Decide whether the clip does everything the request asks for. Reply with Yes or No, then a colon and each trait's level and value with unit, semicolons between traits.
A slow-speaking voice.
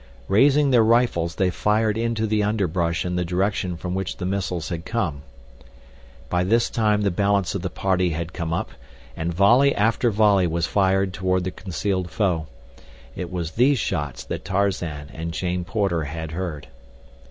No: average, 170 wpm